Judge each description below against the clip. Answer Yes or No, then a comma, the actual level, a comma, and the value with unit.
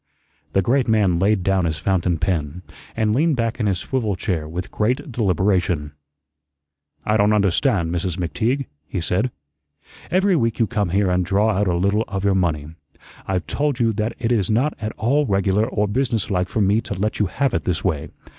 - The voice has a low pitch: Yes, low, 100 Hz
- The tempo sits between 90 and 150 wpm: No, average, 195 wpm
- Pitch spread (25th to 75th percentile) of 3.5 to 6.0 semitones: Yes, average, 4.1 semitones